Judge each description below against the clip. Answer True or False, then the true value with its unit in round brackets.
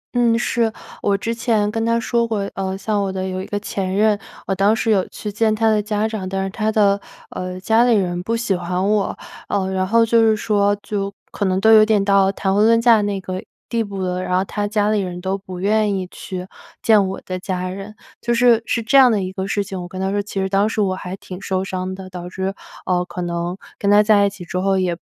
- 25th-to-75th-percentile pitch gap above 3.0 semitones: False (2.5 semitones)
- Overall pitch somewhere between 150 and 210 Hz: True (200 Hz)